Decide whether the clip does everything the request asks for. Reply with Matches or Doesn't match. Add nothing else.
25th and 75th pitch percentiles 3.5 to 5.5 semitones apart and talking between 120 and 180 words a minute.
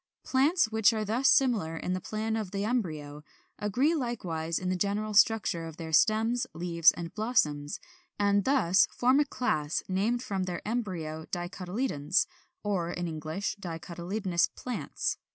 Matches